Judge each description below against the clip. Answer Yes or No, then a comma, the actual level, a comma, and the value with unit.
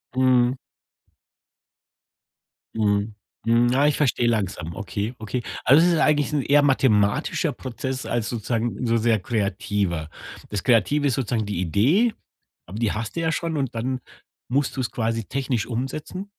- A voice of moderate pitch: No, low, 120 Hz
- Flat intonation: No, average, 4.1 semitones